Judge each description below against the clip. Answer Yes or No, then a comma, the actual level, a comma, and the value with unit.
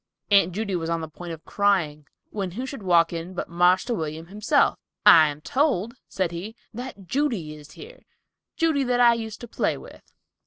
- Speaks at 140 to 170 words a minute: No, average, 190 wpm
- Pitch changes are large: Yes, wide, 6.1 semitones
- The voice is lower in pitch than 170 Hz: No, high, 190 Hz